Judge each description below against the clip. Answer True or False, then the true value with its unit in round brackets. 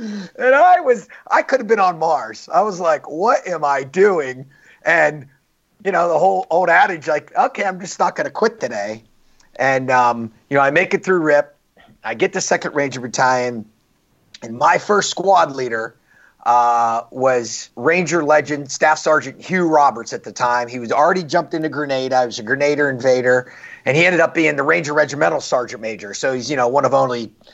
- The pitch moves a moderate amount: False (5.8 semitones)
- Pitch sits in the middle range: True (145 Hz)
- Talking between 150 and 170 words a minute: False (200 wpm)